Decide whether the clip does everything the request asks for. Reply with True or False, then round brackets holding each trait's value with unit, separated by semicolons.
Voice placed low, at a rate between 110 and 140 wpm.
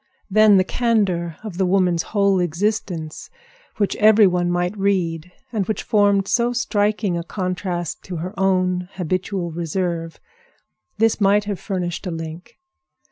False (185 Hz; 135 wpm)